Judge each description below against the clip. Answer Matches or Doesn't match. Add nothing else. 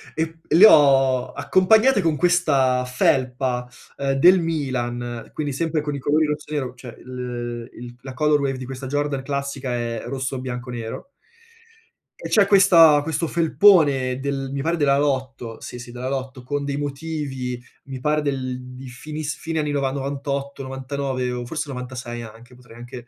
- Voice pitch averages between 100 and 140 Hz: Matches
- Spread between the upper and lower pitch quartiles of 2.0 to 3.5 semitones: Matches